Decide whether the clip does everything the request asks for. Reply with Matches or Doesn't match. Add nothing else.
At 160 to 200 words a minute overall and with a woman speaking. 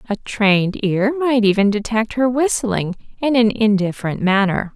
Doesn't match